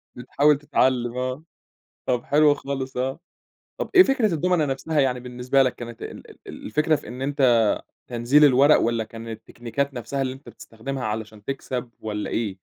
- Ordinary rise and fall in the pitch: Yes, average, 3.2 semitones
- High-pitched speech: No, low, 130 Hz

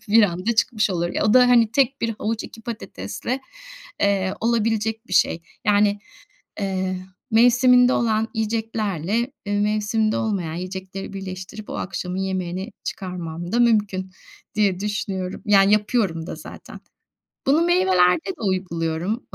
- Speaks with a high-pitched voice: Yes, high, 205 Hz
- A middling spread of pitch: Yes, average, 3.2 semitones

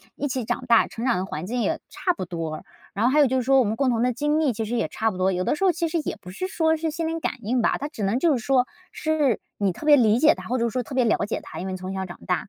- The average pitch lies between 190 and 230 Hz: No, high, 245 Hz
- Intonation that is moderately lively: No, wide, 6.1 semitones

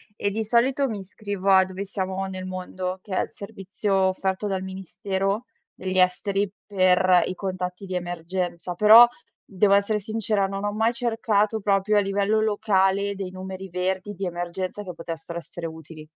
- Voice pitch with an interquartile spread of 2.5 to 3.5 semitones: No, narrow, 1.9 semitones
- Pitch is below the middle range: No, high, 190 Hz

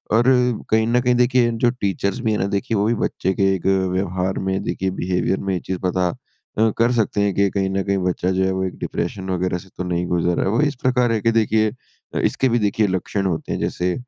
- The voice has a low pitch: Yes, low, 100 Hz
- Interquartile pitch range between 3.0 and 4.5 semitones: Yes, average, 3.6 semitones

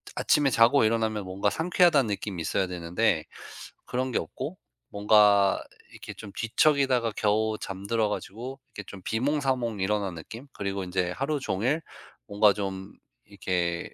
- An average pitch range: Yes, average, 4.3 semitones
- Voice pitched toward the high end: No, low, 105 Hz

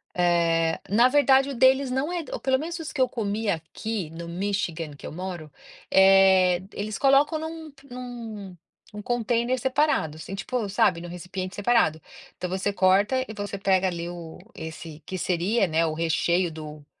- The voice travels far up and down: Yes, wide, 6.3 semitones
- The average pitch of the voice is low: No, high, 195 Hz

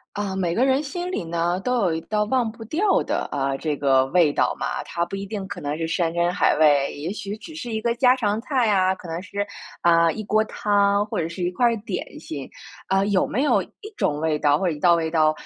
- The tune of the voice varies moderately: Yes, average, 5.0 semitones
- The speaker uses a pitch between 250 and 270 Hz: No, high, 190 Hz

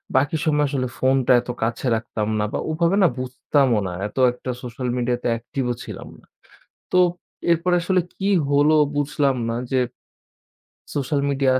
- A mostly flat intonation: No, average, 3.2 semitones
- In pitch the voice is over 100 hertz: Yes, low, 135 Hz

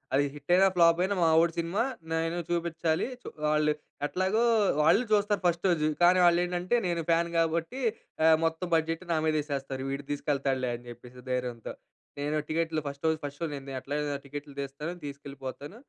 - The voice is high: No, medium, 160 Hz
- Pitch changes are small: No, average, 3.2 semitones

